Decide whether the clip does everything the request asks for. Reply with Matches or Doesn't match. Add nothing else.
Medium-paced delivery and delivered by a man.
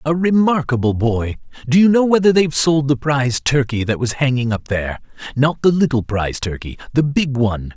Matches